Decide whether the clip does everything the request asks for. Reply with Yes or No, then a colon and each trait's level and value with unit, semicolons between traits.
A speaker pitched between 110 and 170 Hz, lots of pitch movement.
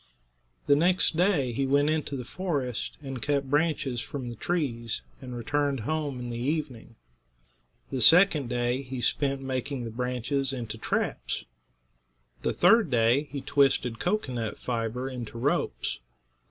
No: low, 135 Hz; average, 3.2 semitones